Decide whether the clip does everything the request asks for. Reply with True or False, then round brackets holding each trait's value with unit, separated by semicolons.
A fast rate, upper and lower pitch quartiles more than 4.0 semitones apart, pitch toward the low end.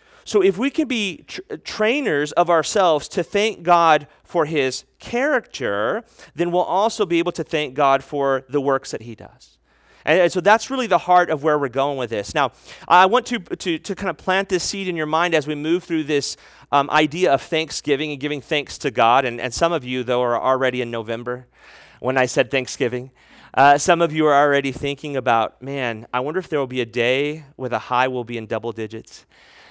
False (220 wpm; 5.3 semitones; 150 Hz)